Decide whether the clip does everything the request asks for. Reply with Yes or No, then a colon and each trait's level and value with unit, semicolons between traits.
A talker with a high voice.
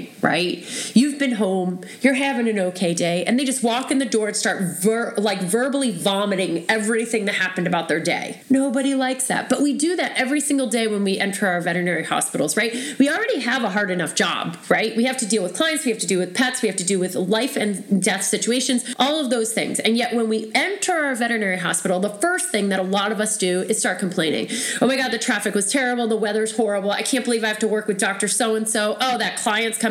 Yes: high, 220 Hz